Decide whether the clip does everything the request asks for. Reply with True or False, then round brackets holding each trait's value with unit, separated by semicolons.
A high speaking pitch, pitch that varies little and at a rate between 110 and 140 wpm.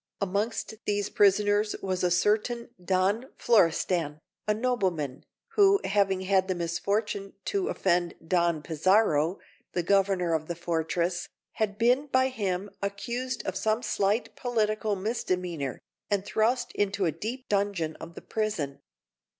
False (200 Hz; 3.9 semitones; 135 wpm)